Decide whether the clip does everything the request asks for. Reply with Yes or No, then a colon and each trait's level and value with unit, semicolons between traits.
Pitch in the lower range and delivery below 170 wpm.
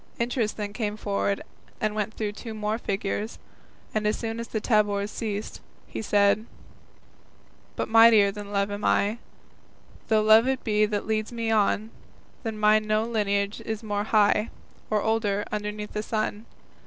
No: high, 215 Hz; average, 160 wpm